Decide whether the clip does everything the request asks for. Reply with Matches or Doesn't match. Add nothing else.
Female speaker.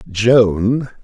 Doesn't match